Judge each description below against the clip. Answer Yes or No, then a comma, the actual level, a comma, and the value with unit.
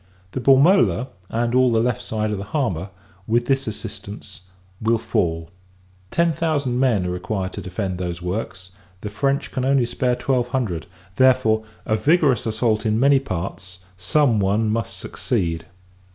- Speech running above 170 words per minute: No, average, 155 wpm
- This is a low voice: Yes, low, 110 Hz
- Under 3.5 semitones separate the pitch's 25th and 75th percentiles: No, average, 5.1 semitones